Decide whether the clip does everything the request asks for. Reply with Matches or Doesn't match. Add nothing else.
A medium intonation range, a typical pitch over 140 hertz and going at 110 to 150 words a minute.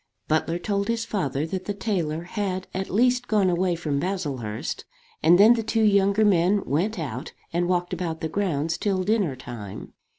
Doesn't match